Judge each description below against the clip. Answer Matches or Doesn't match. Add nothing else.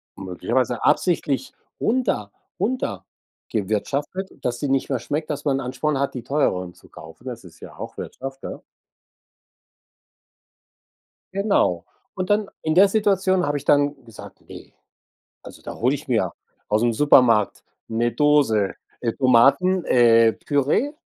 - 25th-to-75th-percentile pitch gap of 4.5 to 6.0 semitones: Matches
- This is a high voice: Doesn't match